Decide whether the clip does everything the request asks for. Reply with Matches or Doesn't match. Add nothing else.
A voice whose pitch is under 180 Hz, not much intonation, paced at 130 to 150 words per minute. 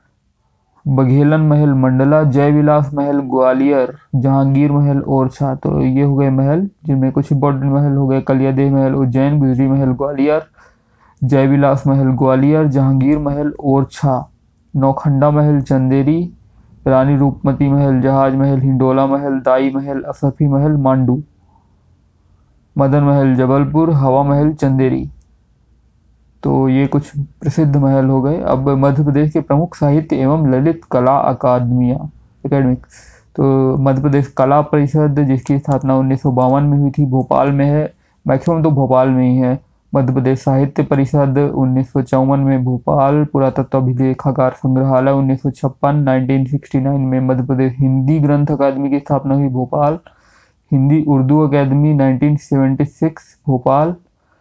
Matches